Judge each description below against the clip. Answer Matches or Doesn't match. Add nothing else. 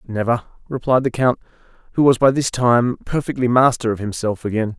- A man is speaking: Matches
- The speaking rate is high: Doesn't match